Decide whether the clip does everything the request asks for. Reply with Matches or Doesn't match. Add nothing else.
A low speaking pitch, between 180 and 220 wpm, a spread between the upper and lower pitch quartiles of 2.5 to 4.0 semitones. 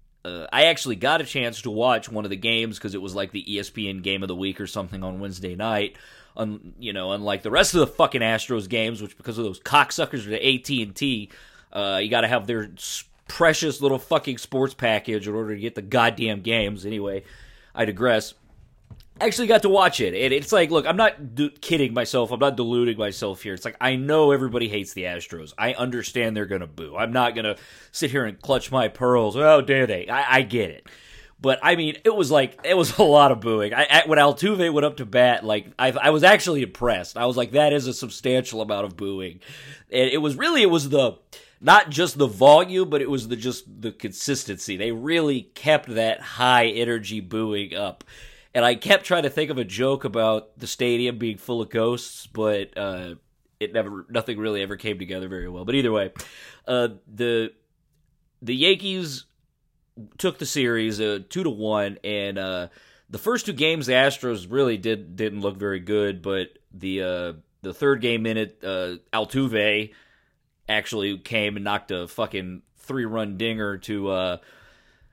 Doesn't match